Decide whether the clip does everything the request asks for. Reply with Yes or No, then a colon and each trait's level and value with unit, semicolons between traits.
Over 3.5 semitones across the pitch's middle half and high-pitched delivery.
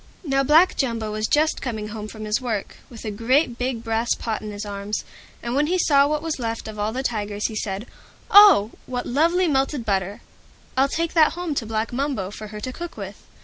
Yes: average, 5.1 semitones; high, 235 Hz